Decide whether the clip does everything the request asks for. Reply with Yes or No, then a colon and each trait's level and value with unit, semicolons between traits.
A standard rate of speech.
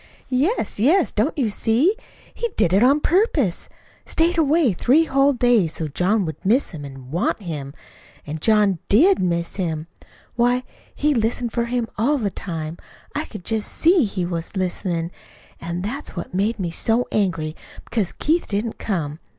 Yes: average, 165 wpm